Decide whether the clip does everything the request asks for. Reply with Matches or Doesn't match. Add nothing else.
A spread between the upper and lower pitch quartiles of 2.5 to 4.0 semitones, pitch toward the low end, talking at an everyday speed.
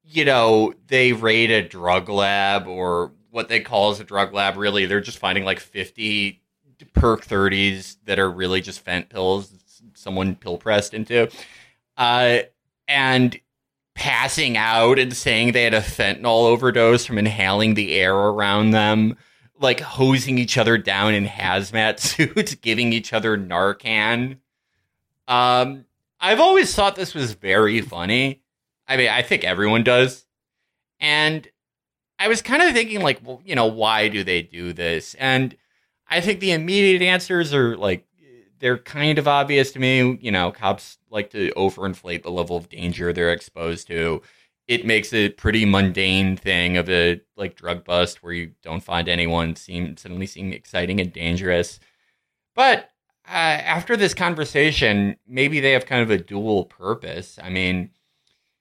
Doesn't match